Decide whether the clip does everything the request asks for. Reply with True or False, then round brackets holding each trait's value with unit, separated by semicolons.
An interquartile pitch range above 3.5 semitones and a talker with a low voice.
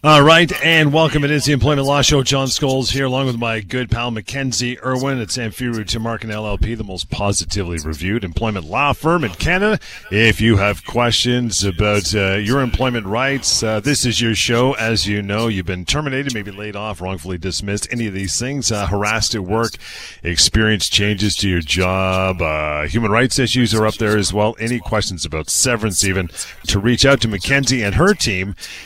True (4.2 semitones; 115 Hz)